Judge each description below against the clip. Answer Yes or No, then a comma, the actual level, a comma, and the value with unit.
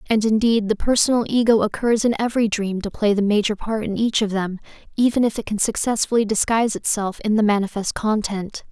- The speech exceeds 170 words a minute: Yes, average, 200 wpm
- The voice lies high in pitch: Yes, high, 215 Hz